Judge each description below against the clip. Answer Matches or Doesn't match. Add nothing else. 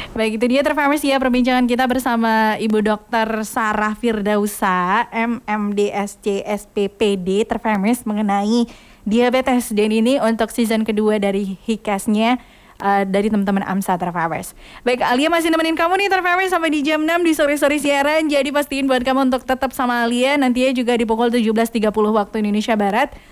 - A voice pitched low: Doesn't match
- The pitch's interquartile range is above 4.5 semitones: Doesn't match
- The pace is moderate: Doesn't match